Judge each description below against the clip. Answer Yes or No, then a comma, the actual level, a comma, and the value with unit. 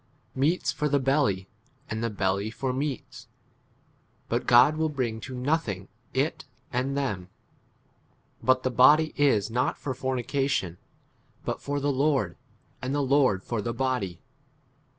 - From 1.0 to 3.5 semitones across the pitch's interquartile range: No, average, 4.3 semitones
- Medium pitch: No, low, 130 Hz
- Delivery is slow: No, average, 145 wpm